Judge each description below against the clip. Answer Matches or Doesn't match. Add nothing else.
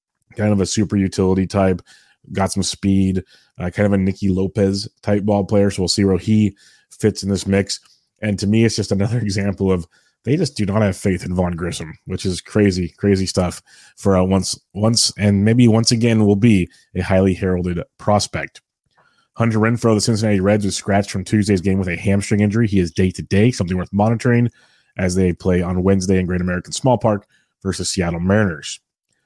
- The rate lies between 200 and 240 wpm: Matches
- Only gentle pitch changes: Matches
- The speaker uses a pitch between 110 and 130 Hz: Doesn't match